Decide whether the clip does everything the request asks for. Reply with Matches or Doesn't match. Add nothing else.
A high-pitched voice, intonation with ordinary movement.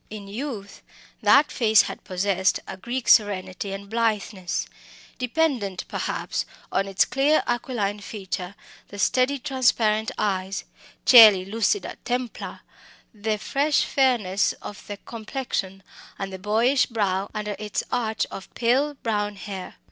Matches